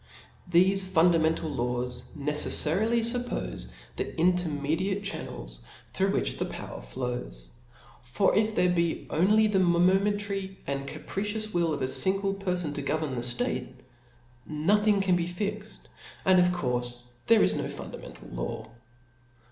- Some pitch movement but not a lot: No, wide, 6.0 semitones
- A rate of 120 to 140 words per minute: Yes, slow, 135 wpm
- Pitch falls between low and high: Yes, medium, 175 Hz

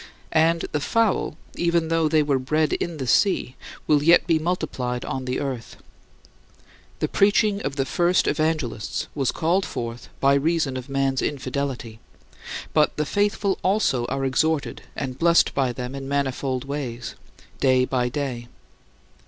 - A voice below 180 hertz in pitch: Yes, medium, 140 Hz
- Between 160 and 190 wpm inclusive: No, average, 150 wpm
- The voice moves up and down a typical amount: Yes, average, 4.1 semitones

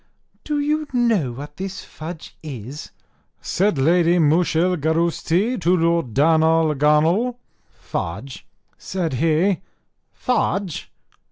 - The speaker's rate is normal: No, slow, 90 wpm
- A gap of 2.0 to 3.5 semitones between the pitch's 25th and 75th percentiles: No, average, 4.0 semitones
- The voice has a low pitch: No, medium, 165 Hz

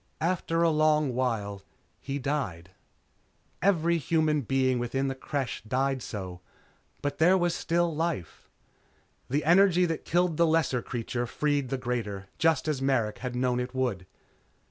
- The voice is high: No, low, 135 Hz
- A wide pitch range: No, average, 4.7 semitones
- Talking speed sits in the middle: Yes, average, 145 wpm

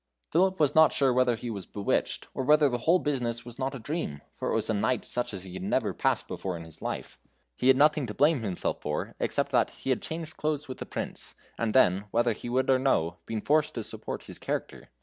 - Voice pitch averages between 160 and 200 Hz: No, low, 125 Hz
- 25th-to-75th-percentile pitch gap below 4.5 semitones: No, wide, 5.5 semitones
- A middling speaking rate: No, fast, 245 wpm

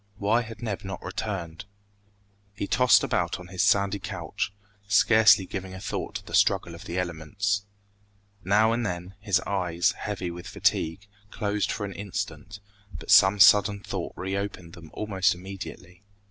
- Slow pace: No, average, 155 wpm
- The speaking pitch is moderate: No, low, 100 Hz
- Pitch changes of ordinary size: No, narrow, 2.3 semitones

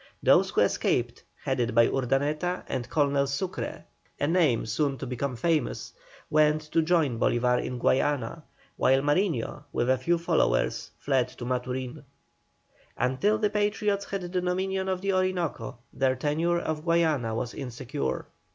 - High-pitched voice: No, medium, 145 Hz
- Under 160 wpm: Yes, average, 145 wpm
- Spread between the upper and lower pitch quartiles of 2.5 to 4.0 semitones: No, wide, 5.4 semitones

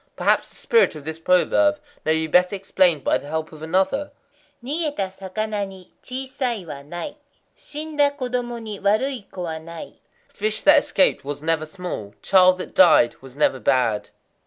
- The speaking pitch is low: No, high, 190 Hz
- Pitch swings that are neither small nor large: No, wide, 7.6 semitones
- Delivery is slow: No, average, 160 wpm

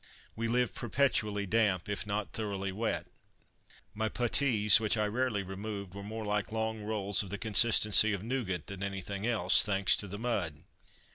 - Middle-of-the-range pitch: No, low, 105 Hz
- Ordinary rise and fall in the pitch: No, narrow, 2.0 semitones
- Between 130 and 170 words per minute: Yes, average, 165 wpm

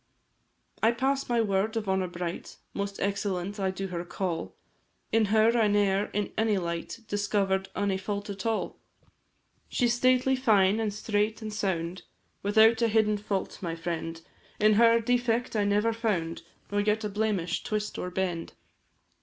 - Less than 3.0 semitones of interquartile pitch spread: Yes, narrow, 2.6 semitones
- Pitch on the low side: No, high, 205 Hz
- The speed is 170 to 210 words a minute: No, average, 160 wpm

